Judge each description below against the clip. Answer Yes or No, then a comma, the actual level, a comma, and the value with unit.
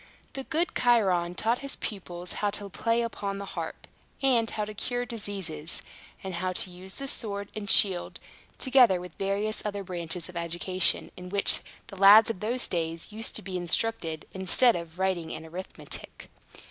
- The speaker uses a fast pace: No, average, 170 wpm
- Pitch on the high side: Yes, high, 195 Hz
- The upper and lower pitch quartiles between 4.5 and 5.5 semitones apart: No, average, 3.9 semitones